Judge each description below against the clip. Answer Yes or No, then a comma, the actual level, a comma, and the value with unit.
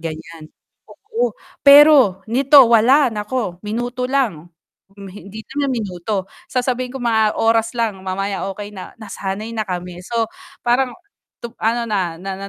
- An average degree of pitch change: Yes, average, 4.5 semitones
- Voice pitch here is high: Yes, high, 220 Hz